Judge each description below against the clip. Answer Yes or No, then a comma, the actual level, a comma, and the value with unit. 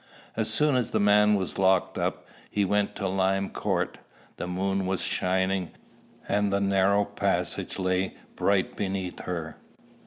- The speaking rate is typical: Yes, average, 150 wpm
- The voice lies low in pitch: Yes, very low, 95 Hz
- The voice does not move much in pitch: Yes, narrow, 1.5 semitones